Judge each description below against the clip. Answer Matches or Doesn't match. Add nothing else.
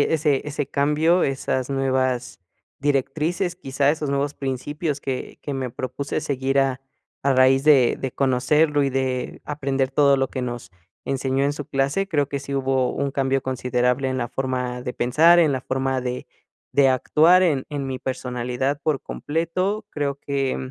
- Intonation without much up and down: Matches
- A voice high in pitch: Doesn't match